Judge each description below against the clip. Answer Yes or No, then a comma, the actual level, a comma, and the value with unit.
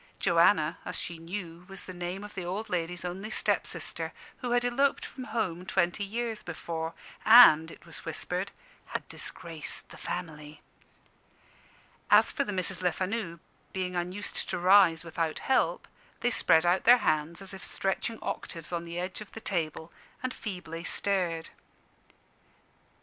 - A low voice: No, medium, 180 Hz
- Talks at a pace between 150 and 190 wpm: Yes, average, 155 wpm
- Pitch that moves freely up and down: No, average, 3.4 semitones